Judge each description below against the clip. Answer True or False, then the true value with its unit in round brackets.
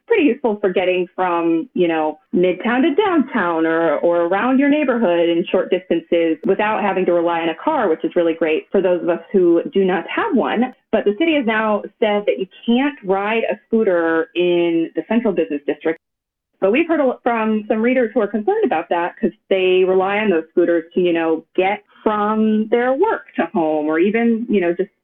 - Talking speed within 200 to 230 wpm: True (205 wpm)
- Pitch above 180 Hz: True (190 Hz)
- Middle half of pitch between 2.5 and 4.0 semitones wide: False (5.0 semitones)